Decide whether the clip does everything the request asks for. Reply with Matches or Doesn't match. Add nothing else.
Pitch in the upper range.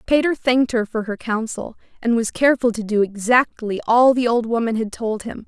Matches